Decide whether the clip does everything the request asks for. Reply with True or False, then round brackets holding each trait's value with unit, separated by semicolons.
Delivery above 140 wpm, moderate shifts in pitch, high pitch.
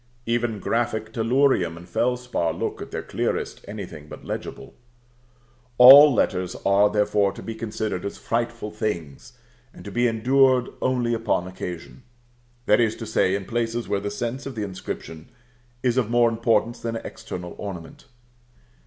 False (155 wpm; 3.2 semitones; 115 Hz)